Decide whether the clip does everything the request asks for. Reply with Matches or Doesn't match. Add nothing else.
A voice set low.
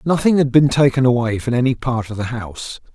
Matches